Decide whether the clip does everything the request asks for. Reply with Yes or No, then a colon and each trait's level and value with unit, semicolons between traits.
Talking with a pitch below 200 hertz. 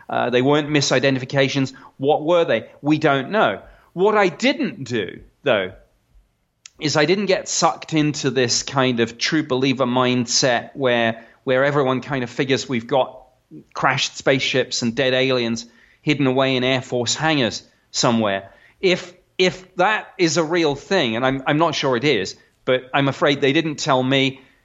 Yes: low, 135 Hz